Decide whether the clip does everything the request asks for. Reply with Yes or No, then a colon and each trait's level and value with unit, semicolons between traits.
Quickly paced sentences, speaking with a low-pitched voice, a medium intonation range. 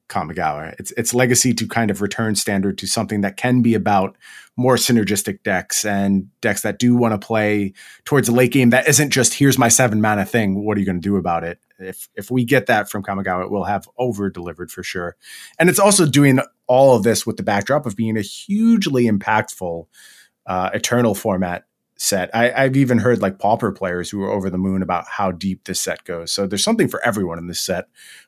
Yes: fast, 220 wpm; low, 105 Hz; average, 4.1 semitones